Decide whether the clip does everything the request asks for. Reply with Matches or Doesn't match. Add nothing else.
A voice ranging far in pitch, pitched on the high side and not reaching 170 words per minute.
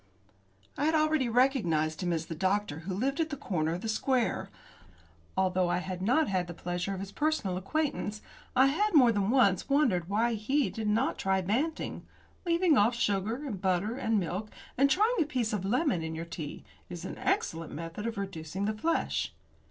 Doesn't match